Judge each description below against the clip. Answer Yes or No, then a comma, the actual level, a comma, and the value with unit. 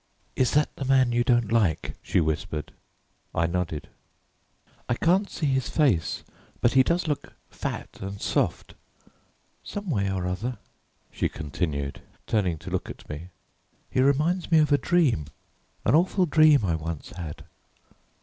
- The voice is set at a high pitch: No, low, 120 Hz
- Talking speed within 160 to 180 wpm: No, average, 150 wpm